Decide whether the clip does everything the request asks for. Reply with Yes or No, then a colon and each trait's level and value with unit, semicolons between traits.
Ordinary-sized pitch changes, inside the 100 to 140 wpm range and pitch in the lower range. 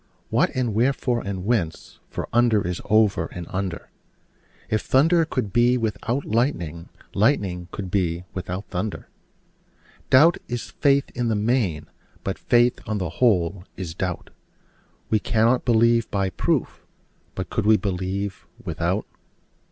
Yes: average, 4.5 semitones; slow, 135 wpm; low, 105 Hz